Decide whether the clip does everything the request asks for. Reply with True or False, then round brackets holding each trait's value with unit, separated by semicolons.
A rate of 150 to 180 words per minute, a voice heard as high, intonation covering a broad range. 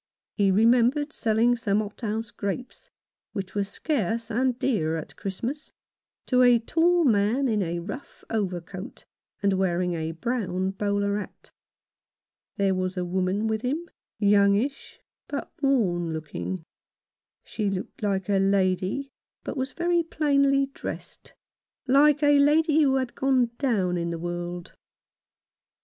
False (140 wpm; 215 Hz; 5.9 semitones)